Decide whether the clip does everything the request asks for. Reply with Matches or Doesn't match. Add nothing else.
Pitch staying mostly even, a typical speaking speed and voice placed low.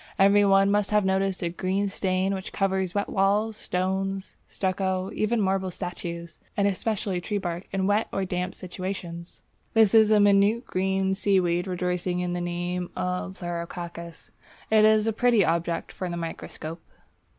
Doesn't match